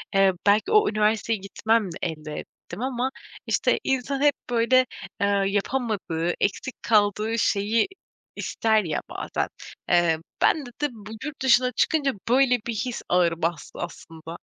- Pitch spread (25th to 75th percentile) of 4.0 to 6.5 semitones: Yes, average, 4.9 semitones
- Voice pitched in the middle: No, high, 220 Hz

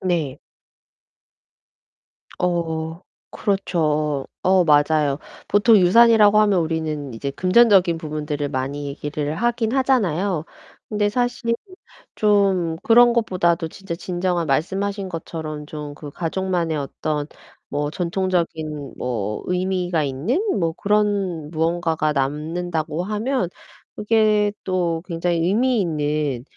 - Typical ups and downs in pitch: Yes, average, 4.5 semitones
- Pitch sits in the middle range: Yes, medium, 170 Hz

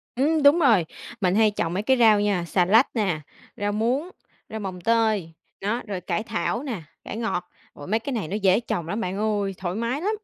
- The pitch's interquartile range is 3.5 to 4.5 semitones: Yes, average, 3.8 semitones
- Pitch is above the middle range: Yes, high, 210 Hz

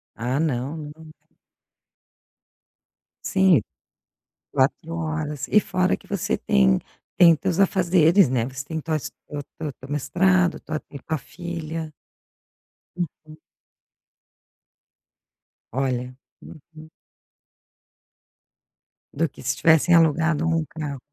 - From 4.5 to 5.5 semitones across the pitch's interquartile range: No, average, 2.9 semitones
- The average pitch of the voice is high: No, medium, 155 Hz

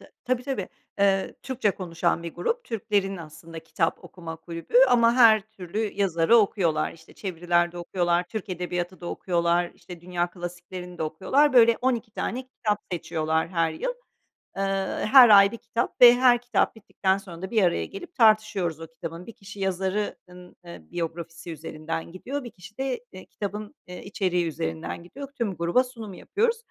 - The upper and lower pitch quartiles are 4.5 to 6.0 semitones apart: Yes, average, 4.8 semitones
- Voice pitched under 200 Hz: Yes, high, 190 Hz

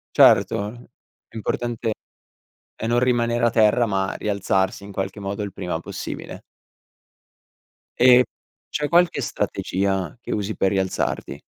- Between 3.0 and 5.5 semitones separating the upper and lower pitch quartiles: Yes, average, 3.7 semitones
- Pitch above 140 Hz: No, low, 105 Hz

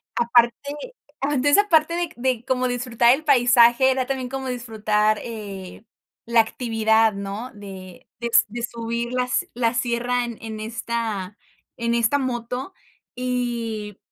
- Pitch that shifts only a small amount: Yes, narrow, 2.2 semitones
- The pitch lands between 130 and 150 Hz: No, high, 235 Hz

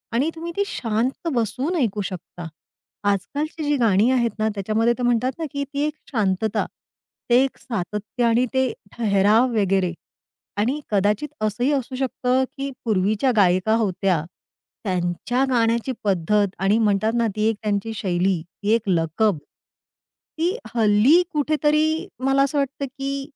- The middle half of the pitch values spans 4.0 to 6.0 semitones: Yes, average, 5.0 semitones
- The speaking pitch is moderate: No, high, 225 Hz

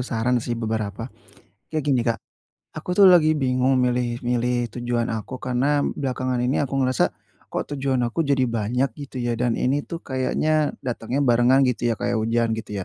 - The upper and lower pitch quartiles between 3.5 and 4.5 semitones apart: No, narrow, 2.5 semitones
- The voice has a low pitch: Yes, low, 125 Hz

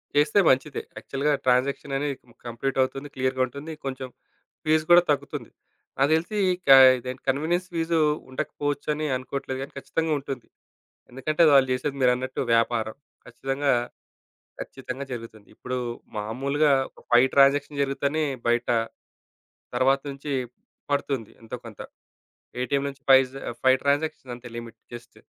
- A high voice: No, low, 135 Hz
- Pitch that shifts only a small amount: Yes, narrow, 2.2 semitones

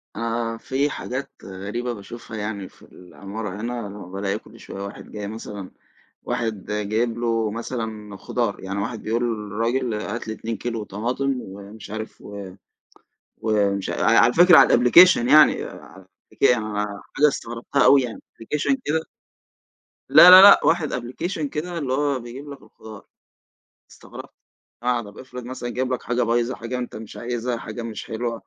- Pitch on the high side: No, low, 115 Hz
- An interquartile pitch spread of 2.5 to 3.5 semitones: Yes, average, 3.1 semitones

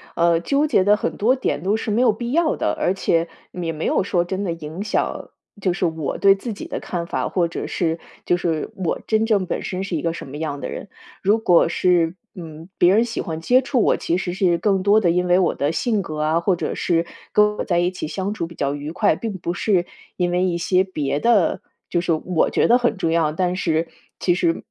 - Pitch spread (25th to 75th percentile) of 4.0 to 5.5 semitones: No, average, 3.4 semitones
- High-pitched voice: No, medium, 180 Hz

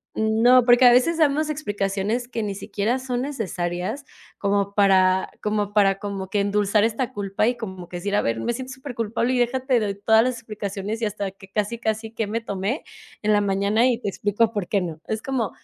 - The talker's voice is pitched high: Yes, high, 215 Hz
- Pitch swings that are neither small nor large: Yes, average, 3.2 semitones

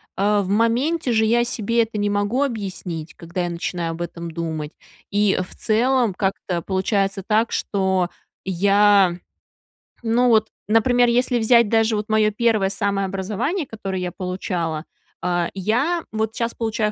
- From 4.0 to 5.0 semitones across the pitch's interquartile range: No, average, 3.5 semitones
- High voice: Yes, high, 205 Hz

